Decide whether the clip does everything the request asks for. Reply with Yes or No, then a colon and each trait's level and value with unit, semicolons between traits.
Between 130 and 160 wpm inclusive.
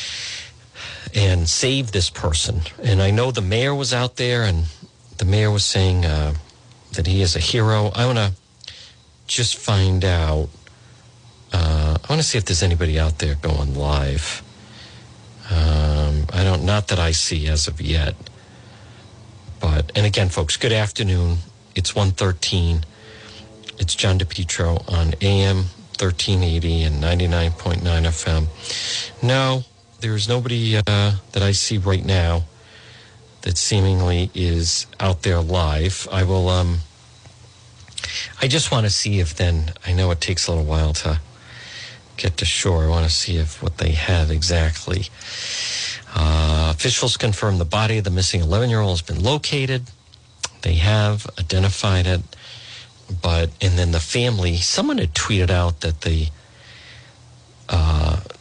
Yes: average, 150 wpm